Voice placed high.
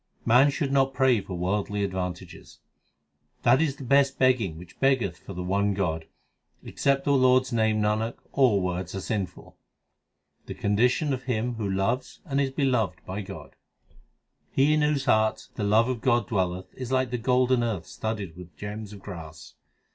No: low, 110 Hz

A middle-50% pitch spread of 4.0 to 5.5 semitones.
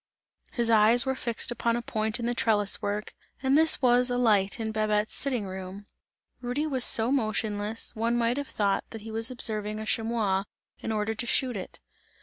No: narrow, 2.4 semitones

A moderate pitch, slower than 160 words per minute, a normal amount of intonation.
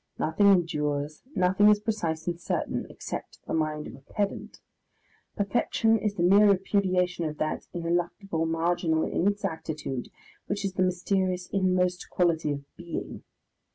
Yes: medium, 180 Hz; slow, 135 wpm; average, 3.5 semitones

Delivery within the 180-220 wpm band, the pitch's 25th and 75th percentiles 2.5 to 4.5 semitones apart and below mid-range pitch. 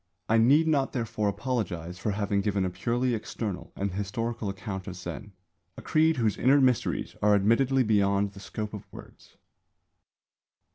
No: average, 155 wpm; average, 3.6 semitones; low, 105 Hz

